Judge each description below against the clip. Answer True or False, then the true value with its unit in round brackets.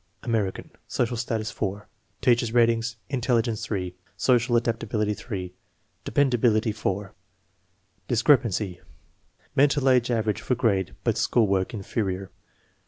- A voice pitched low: True (115 Hz)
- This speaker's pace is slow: True (110 wpm)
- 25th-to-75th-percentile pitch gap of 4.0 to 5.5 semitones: False (3.0 semitones)